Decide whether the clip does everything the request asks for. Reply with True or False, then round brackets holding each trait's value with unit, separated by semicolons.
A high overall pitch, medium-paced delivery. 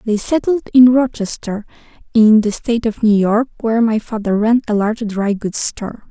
True (225 Hz; 185 wpm)